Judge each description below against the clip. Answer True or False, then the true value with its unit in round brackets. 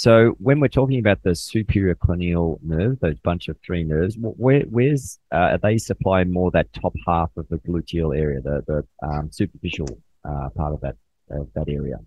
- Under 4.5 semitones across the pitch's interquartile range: False (5.3 semitones)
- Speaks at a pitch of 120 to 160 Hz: False (85 Hz)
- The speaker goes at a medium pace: True (190 wpm)